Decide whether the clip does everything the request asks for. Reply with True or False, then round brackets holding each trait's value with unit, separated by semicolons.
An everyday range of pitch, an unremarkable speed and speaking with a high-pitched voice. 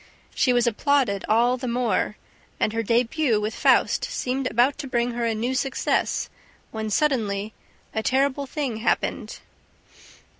True (3.1 semitones; 145 wpm; 240 Hz)